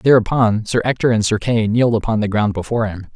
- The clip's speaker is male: Yes, male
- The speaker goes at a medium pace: No, fast, 230 wpm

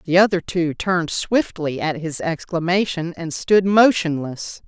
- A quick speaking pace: No, average, 140 wpm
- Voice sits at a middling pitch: Yes, medium, 170 Hz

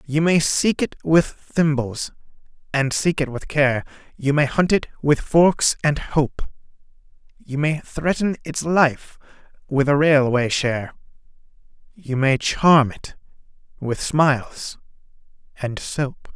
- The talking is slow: Yes, slow, 130 wpm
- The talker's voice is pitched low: No, medium, 145 Hz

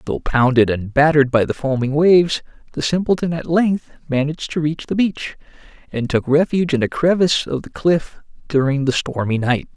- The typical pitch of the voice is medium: Yes, medium, 150 Hz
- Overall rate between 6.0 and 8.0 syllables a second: No, 5.4 syllables/s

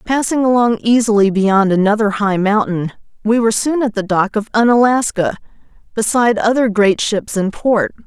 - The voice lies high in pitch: Yes, high, 215 Hz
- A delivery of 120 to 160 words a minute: Yes, average, 155 wpm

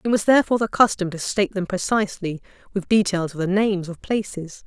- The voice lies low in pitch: No, high, 195 Hz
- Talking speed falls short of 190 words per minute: No, fast, 205 wpm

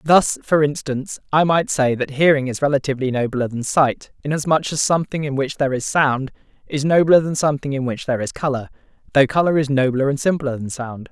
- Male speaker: Yes, male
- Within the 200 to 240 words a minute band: Yes, fast, 205 wpm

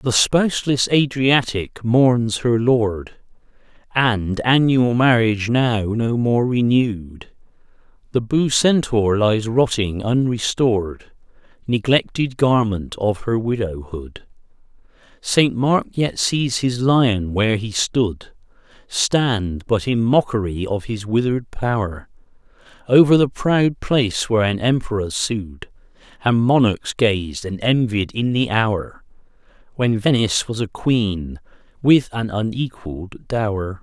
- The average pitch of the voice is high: No, low, 115 Hz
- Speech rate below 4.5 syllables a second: Yes, 3.8 syllables/s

